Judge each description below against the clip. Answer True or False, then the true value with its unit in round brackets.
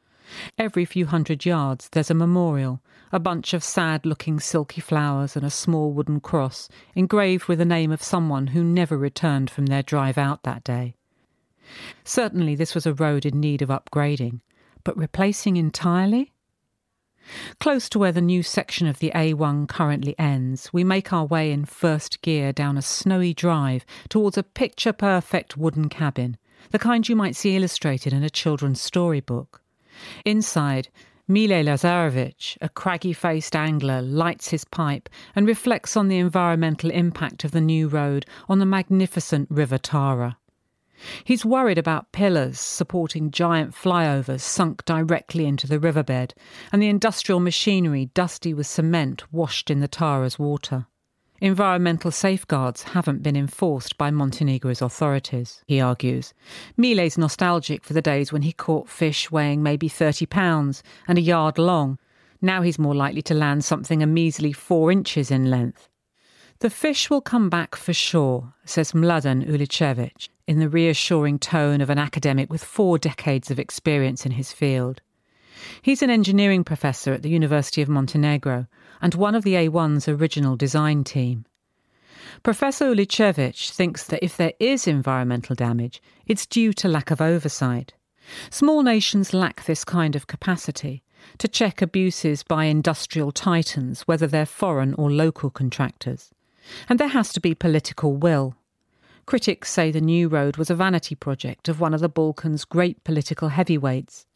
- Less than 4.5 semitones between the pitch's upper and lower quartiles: True (3.9 semitones)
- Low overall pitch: False (160 Hz)